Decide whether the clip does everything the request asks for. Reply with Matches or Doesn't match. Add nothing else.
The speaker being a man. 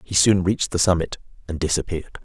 Matches